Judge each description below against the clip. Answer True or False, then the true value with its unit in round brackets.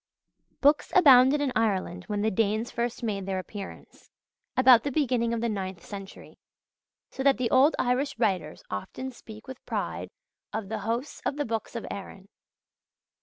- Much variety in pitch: False (4.5 semitones)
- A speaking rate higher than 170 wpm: False (165 wpm)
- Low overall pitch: False (230 Hz)